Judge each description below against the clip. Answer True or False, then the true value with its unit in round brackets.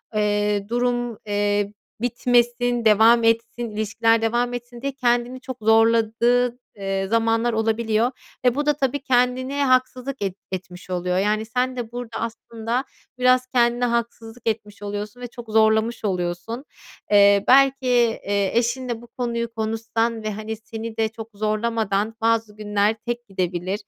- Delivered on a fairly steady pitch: True (2.3 semitones)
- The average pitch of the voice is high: True (230 Hz)